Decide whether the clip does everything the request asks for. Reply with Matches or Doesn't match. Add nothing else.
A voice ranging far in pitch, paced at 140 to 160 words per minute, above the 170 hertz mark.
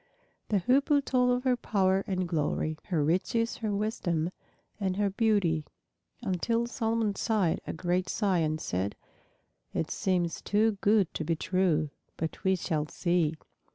Doesn't match